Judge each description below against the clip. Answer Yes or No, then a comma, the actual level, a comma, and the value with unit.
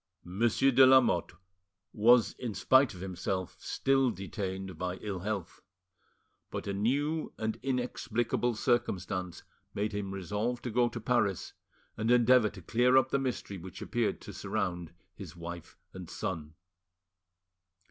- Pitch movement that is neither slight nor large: Yes, average, 4.7 semitones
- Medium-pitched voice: No, low, 105 Hz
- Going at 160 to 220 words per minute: No, slow, 135 wpm